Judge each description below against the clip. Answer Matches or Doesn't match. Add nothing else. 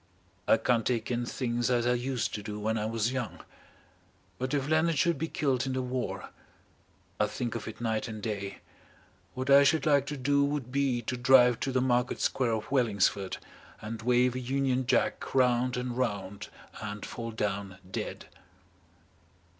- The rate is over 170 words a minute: Matches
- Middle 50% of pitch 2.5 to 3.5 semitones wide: Matches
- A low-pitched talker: Matches